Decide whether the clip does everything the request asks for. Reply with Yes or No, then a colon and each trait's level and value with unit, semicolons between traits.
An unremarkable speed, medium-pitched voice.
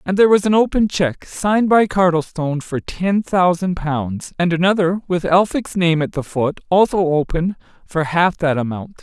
Yes: average, 180 wpm; medium, 175 Hz